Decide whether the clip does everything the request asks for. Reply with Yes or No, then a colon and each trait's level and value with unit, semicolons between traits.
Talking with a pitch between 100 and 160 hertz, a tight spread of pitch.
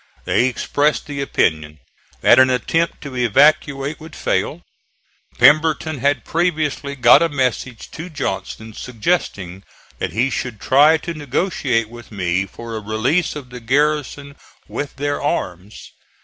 No: low, 135 Hz; average, 4.7 semitones